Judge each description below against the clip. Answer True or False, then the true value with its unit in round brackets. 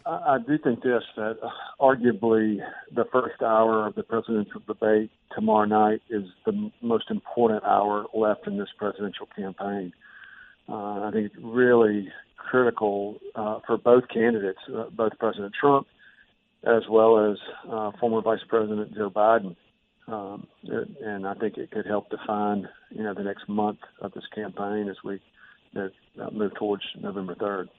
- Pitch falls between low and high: False (110 Hz)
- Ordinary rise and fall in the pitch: False (1.9 semitones)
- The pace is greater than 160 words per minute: False (155 wpm)